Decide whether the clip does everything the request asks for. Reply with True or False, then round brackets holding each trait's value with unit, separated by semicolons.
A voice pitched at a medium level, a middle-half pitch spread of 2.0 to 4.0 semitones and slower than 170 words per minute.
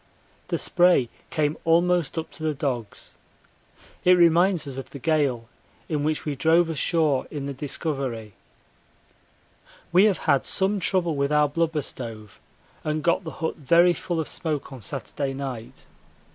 True (155 Hz; 3.7 semitones; 155 wpm)